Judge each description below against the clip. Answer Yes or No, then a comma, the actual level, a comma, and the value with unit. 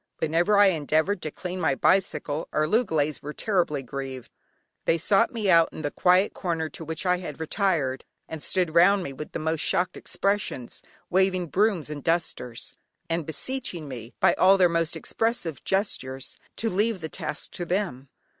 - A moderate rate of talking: Yes, average, 175 wpm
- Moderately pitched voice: Yes, medium, 170 Hz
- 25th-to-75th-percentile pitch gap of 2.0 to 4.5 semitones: Yes, average, 4.1 semitones